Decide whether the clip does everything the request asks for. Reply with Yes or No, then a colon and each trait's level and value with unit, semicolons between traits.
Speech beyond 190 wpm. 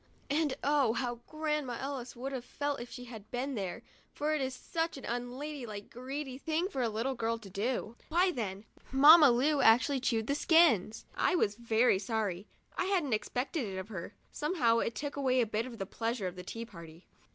Yes: average, 200 wpm